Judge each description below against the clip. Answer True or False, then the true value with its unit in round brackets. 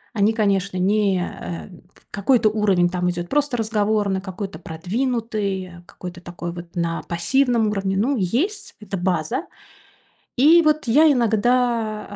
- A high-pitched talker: True (205 Hz)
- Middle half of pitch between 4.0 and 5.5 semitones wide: True (4.7 semitones)